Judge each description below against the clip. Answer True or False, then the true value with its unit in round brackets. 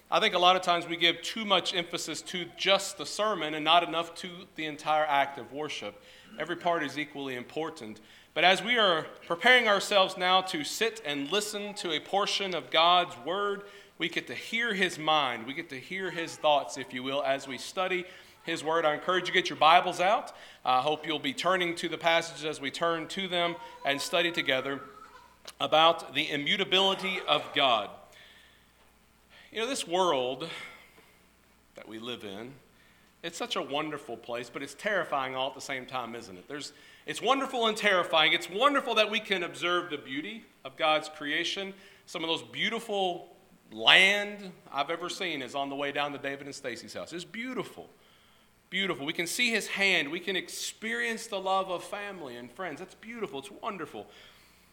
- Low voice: False (170 Hz)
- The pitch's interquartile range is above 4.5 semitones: True (5.2 semitones)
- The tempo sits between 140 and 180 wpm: False (190 wpm)